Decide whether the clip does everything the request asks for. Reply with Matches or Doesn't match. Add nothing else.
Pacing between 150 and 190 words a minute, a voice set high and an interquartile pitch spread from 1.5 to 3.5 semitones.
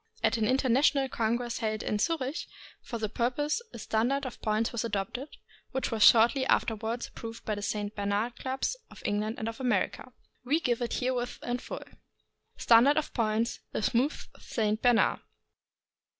Matches